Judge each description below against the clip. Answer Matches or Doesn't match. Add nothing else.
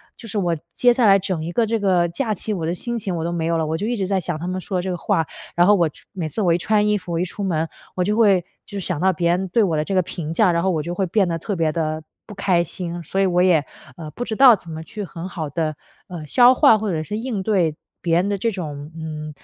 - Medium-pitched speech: Matches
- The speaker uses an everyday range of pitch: Matches